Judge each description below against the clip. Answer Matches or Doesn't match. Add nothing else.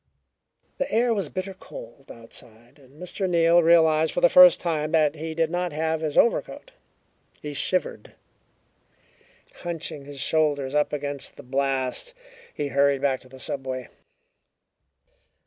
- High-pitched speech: Doesn't match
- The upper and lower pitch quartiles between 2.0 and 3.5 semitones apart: Doesn't match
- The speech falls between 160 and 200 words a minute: Doesn't match